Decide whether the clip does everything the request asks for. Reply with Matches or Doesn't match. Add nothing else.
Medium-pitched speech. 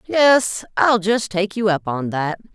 Doesn't match